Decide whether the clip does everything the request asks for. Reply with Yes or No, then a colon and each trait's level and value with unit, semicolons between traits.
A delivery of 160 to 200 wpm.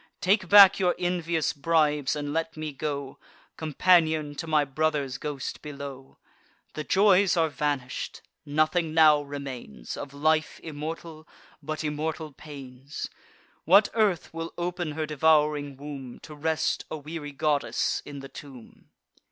No: slow, 135 wpm